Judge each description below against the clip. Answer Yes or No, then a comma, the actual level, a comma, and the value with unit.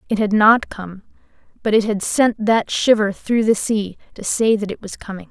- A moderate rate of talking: No, fast, 215 wpm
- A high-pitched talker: Yes, high, 210 Hz